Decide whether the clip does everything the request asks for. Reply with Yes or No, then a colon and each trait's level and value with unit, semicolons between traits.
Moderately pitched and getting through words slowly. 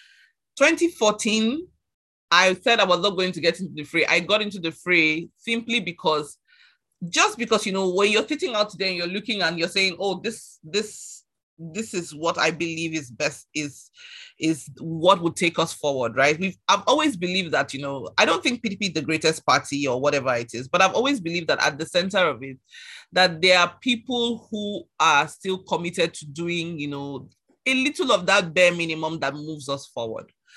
No: medium, 175 Hz; average, 200 wpm